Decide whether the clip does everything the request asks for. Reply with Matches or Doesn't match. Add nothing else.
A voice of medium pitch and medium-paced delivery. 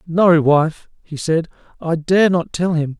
Matches